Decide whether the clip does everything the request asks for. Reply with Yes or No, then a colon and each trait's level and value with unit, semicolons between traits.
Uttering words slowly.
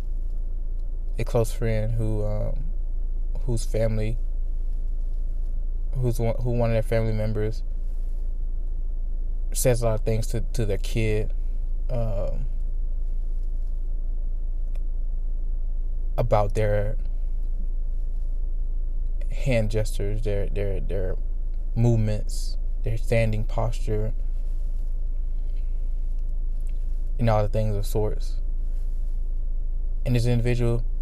Yes: slow, 90 wpm